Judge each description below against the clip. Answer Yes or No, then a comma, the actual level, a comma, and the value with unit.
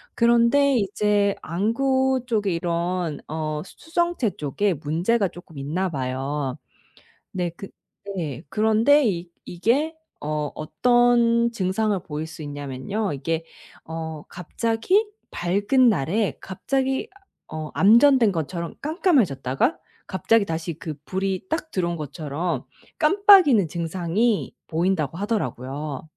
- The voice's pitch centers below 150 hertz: No, medium, 185 Hz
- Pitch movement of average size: No, wide, 6.7 semitones